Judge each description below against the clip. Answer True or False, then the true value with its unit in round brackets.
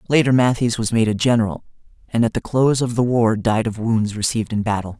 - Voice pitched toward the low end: True (115 Hz)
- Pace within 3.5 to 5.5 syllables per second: False (6.2 syllables/s)